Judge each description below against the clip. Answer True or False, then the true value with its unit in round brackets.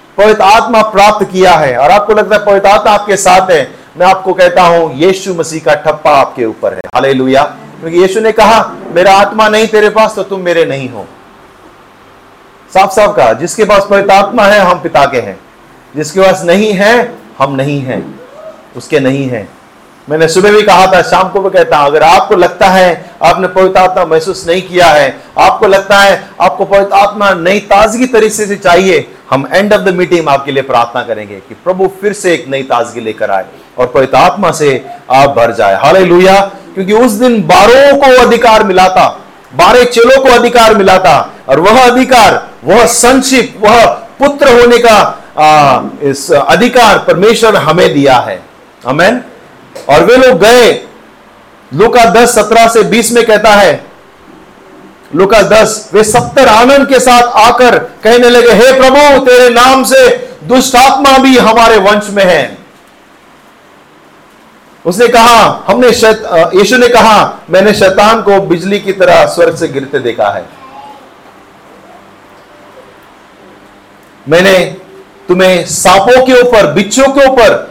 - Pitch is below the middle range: False (200 Hz)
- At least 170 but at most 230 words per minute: False (160 wpm)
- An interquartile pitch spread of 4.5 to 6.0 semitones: True (4.8 semitones)